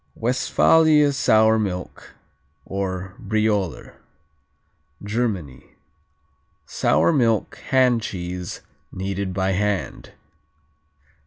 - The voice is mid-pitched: No, low, 100 Hz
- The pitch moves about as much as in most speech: Yes, average, 3.7 semitones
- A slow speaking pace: Yes, slow, 70 wpm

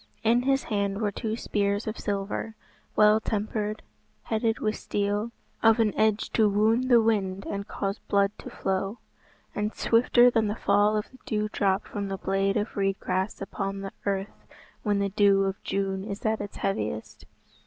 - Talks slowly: No, average, 175 wpm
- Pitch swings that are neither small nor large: No, narrow, 1.7 semitones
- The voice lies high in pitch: Yes, high, 205 Hz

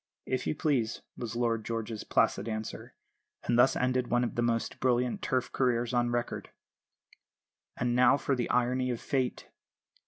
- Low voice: Yes, low, 120 Hz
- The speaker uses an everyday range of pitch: No, narrow, 1.4 semitones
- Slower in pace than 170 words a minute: Yes, average, 160 wpm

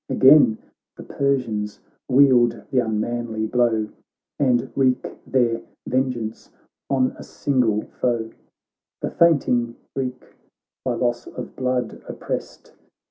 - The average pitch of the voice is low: Yes, low, 120 Hz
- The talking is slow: Yes, slow, 110 wpm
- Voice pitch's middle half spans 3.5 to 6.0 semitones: No, narrow, 2.4 semitones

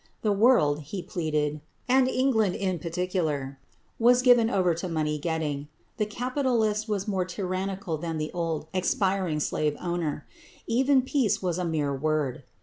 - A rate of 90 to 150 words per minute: Yes, average, 145 wpm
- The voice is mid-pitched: Yes, medium, 180 Hz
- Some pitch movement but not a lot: No, wide, 5.7 semitones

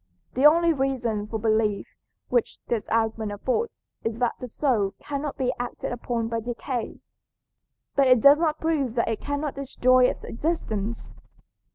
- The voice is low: No, high, 245 Hz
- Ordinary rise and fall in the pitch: Yes, average, 3.9 semitones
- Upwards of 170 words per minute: No, average, 155 wpm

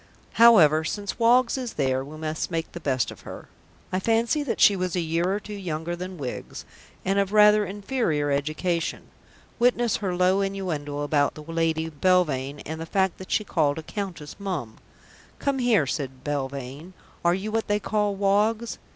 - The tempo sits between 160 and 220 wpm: Yes, average, 175 wpm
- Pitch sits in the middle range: Yes, medium, 180 Hz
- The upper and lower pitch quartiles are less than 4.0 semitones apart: No, average, 5.3 semitones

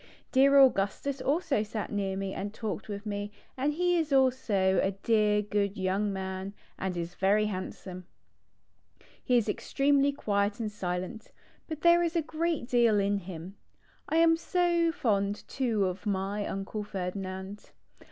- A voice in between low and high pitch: No, high, 210 Hz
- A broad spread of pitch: Yes, wide, 5.9 semitones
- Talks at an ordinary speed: Yes, average, 155 wpm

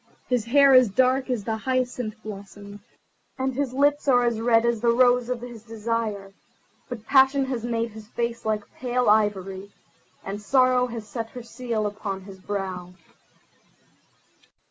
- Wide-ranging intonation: No, average, 3.2 semitones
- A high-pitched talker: Yes, high, 230 Hz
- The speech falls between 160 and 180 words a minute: No, average, 150 wpm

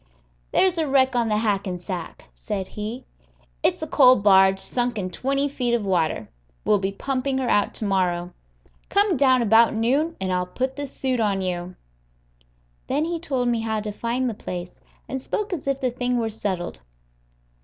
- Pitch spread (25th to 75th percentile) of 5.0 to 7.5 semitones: Yes, wide, 5.5 semitones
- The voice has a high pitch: Yes, high, 230 Hz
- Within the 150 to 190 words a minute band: Yes, average, 180 wpm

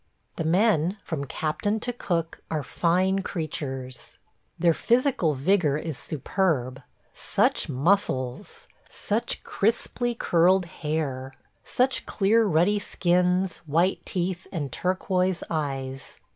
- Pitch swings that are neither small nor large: Yes, average, 4.5 semitones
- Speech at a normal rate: No, slow, 110 wpm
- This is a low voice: No, medium, 175 Hz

